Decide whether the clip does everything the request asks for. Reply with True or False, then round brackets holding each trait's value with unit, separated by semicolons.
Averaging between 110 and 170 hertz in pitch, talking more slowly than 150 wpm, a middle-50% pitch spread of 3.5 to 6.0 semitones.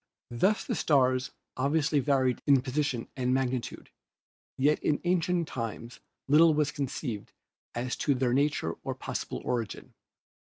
False (135 Hz; 140 wpm; 3.1 semitones)